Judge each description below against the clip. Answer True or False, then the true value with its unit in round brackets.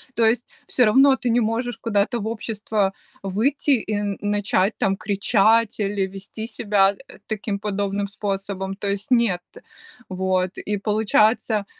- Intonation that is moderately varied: False (2.3 semitones)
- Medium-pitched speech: False (205 Hz)